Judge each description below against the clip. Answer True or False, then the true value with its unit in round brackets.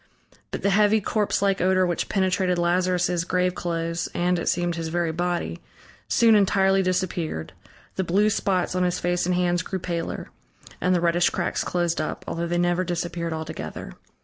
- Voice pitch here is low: False (175 Hz)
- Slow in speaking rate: False (170 wpm)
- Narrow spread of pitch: True (1.5 semitones)